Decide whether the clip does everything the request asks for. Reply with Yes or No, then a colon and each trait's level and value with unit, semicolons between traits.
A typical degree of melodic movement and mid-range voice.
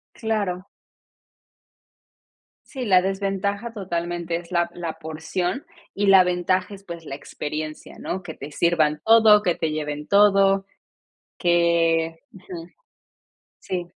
Yes: average, 3.1 semitones; medium, 175 Hz